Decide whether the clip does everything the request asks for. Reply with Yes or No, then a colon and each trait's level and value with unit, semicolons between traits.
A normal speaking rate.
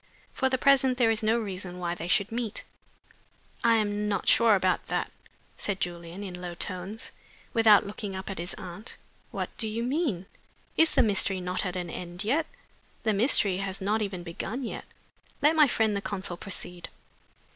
Yes: average, 180 wpm